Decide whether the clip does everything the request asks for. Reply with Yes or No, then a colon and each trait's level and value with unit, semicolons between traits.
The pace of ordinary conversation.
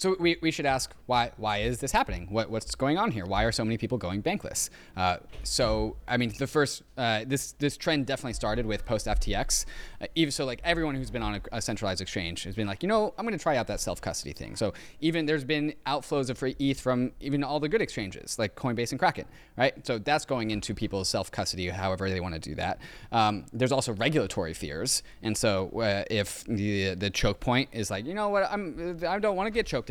No: fast, 240 wpm